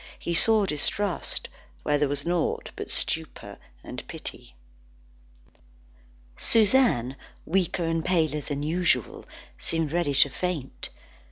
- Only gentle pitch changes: No, average, 3.8 semitones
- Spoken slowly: Yes, slow, 110 wpm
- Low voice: No, medium, 165 Hz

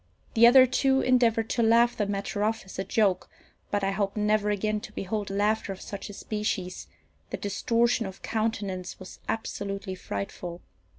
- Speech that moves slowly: No, average, 170 wpm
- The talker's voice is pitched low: No, high, 210 Hz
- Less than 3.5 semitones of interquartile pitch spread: Yes, narrow, 2.5 semitones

